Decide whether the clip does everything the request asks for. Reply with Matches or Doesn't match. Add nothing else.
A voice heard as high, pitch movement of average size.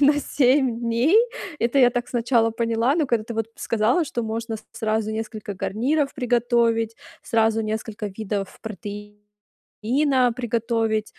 Doesn't match